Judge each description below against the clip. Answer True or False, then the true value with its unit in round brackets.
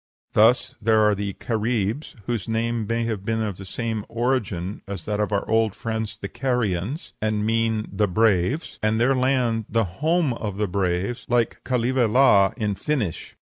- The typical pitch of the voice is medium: False (110 Hz)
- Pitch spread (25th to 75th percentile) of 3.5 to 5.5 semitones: False (2.6 semitones)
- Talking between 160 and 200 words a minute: True (165 wpm)